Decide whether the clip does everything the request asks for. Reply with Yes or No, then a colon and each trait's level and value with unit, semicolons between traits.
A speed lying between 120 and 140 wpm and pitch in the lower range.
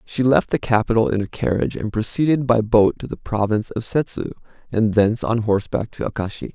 No: average, 200 wpm; low, 110 Hz